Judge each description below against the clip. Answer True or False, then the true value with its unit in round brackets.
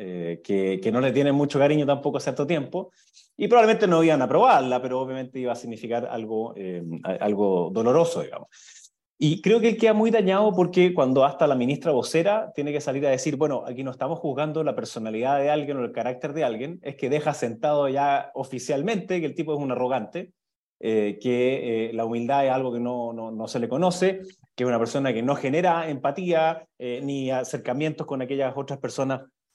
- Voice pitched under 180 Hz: True (140 Hz)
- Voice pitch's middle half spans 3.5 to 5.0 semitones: True (4.0 semitones)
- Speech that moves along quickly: True (205 wpm)